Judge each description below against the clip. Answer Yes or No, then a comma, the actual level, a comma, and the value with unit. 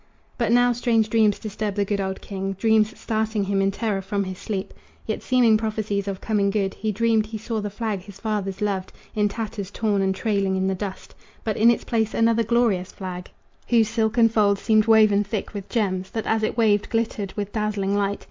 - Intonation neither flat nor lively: No, narrow, 2.1 semitones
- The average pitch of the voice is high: Yes, high, 210 Hz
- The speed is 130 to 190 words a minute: No, fast, 205 wpm